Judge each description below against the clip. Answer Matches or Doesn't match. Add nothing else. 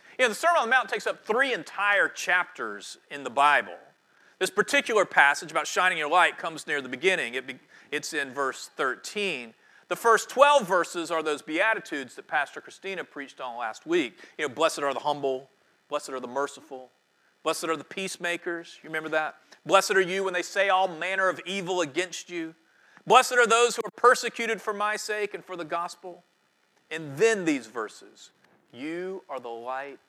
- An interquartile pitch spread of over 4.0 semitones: Matches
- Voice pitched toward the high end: Doesn't match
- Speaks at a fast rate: Doesn't match